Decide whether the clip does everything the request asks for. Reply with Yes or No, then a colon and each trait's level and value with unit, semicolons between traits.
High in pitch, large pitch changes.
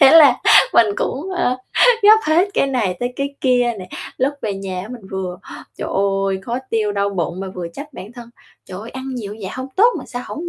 Yes: high, 235 Hz; wide, 5.7 semitones